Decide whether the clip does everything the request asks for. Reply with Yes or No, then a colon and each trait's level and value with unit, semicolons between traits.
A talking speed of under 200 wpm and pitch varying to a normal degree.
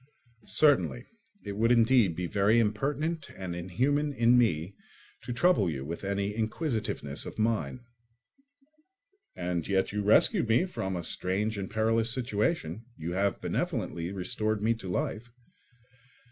Yes: slow, 135 wpm; average, 4.1 semitones